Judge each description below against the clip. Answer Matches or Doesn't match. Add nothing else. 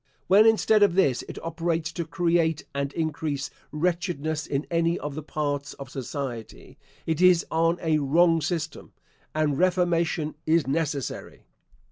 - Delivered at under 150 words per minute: Matches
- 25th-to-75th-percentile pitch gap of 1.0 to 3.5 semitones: Matches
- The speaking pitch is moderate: Matches